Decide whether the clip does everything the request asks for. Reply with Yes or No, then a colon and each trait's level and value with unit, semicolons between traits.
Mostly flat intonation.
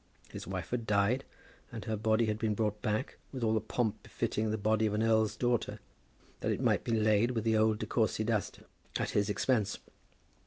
Yes: narrow, 1.2 semitones